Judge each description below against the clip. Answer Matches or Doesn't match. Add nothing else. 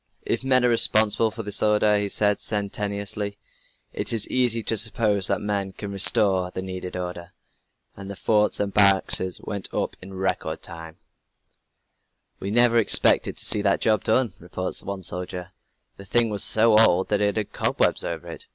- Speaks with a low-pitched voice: Matches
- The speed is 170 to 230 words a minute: Matches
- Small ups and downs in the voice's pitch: Matches